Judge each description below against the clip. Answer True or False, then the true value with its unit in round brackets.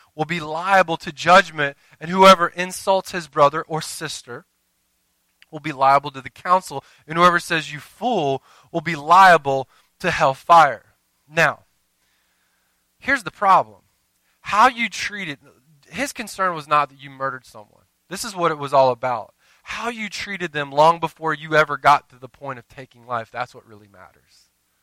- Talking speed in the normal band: True (170 wpm)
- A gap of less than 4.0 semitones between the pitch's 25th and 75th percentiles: False (4.8 semitones)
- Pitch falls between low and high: True (150 Hz)